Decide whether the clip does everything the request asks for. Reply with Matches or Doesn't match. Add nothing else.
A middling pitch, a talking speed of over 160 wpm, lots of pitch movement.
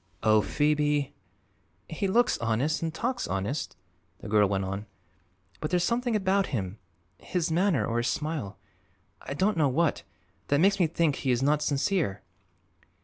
Doesn't match